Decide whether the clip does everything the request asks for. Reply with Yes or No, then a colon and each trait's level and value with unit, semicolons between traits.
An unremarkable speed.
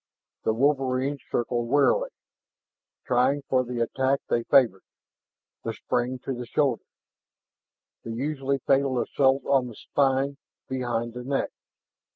No: slow, 125 wpm